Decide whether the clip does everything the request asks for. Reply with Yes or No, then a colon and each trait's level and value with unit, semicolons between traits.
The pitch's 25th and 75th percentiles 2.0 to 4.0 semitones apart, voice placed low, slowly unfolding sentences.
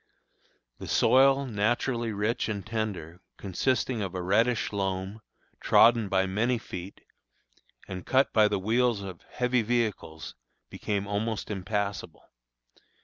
Yes: average, 3.5 semitones; low, 105 Hz; slow, 120 wpm